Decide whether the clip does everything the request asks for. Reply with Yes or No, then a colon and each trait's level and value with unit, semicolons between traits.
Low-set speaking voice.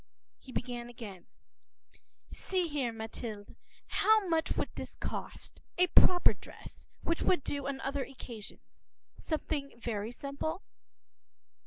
No: very high, 275 Hz